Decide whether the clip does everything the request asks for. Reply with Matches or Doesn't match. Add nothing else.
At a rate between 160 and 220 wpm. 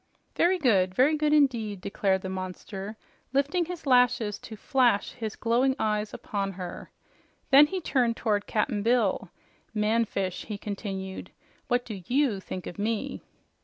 Doesn't match